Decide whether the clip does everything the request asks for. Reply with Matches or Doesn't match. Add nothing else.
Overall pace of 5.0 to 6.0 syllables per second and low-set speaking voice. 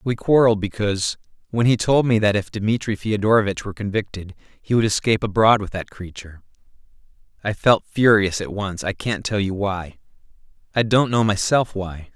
Matches